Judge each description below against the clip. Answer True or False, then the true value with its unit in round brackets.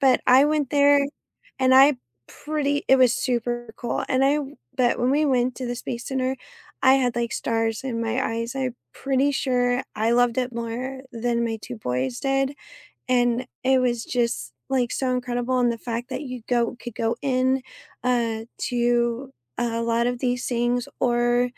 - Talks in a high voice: True (245 Hz)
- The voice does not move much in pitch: True (1.8 semitones)